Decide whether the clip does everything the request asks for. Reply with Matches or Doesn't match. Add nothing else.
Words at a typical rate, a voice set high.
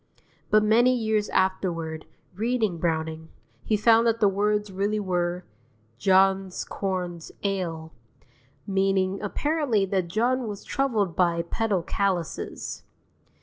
Doesn't match